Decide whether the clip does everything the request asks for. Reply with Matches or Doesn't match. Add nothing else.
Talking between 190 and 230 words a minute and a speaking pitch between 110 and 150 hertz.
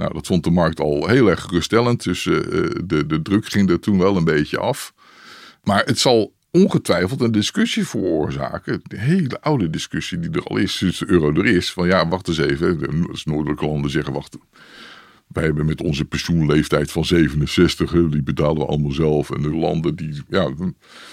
Doesn't match